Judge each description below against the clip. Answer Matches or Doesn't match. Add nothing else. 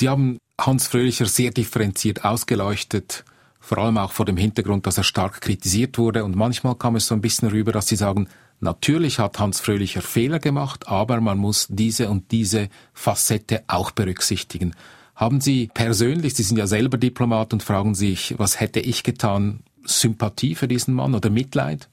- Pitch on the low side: Matches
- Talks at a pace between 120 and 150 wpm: Doesn't match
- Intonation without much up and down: Doesn't match